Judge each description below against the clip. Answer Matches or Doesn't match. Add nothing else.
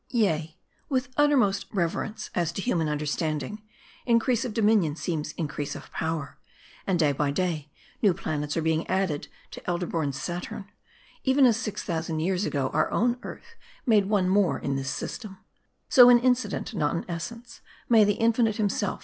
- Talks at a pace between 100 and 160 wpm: Doesn't match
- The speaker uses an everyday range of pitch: Doesn't match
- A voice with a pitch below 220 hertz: Matches